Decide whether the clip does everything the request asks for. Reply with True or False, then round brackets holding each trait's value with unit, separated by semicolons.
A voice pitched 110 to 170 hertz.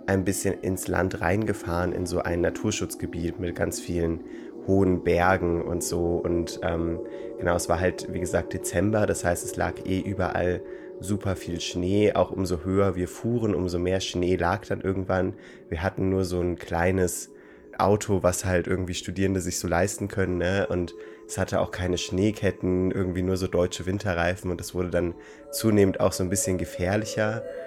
False (90 Hz)